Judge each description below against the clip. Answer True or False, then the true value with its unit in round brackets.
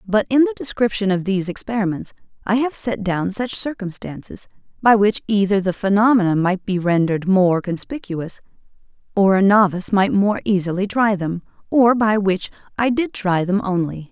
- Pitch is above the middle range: True (200 Hz)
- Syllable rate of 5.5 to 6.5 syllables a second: False (5.1 syllables/s)